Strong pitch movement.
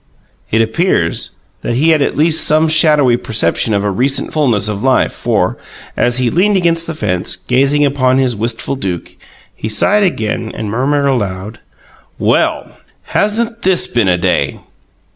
Yes: wide, 6.3 semitones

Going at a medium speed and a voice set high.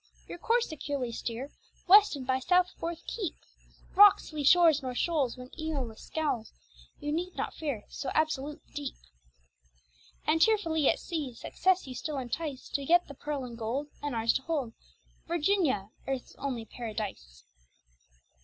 Yes: average, 155 wpm; very high, 290 Hz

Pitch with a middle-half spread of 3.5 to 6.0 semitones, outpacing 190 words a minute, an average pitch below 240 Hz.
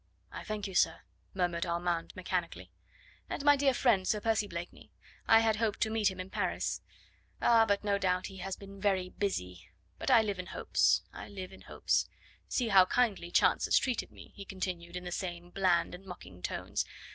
No: average, 3.1 semitones; average, 200 wpm; high, 190 Hz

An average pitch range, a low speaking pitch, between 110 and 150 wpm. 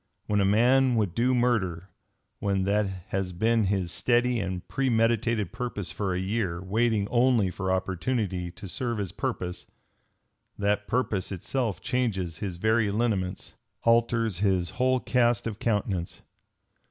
Yes: average, 4.0 semitones; low, 105 Hz; average, 140 wpm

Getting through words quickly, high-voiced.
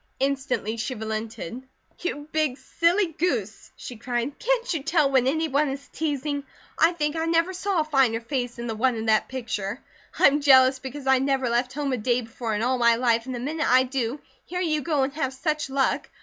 Yes: fast, 210 wpm; very high, 265 Hz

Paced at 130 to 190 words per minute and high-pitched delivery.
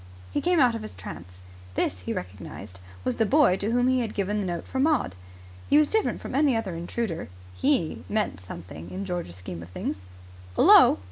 No: average, 200 wpm; high, 200 Hz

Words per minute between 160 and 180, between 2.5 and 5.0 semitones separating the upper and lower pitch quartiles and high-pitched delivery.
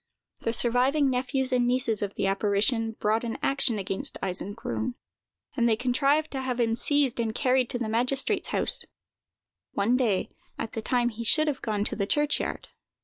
Yes: average, 175 wpm; average, 3.0 semitones; high, 240 Hz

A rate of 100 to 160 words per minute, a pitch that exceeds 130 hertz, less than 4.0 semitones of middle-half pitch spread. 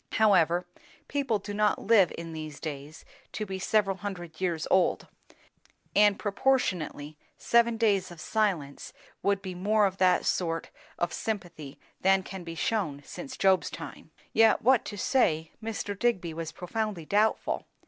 No: average, 150 wpm; high, 190 Hz; average, 4.3 semitones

